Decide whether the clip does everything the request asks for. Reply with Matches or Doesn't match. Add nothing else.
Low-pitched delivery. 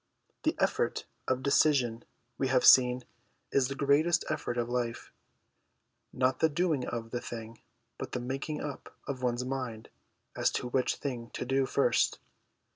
Matches